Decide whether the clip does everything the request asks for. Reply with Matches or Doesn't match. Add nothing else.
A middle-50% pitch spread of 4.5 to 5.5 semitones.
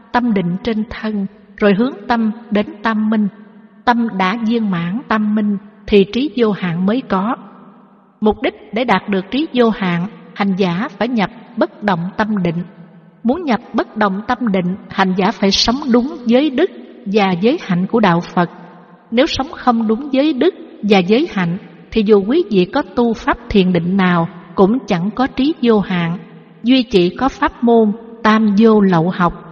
Doesn't match